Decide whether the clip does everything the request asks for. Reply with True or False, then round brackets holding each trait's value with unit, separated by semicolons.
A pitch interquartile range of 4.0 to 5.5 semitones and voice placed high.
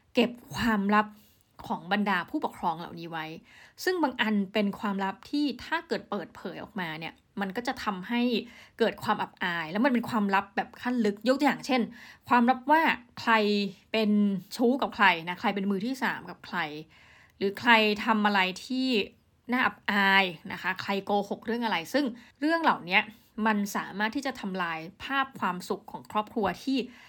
False (3.6 semitones; 215 Hz)